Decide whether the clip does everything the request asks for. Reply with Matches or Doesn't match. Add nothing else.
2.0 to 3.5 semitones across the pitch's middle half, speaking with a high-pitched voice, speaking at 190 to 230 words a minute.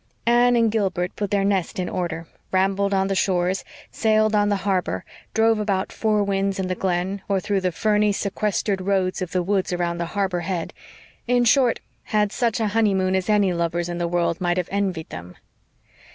Matches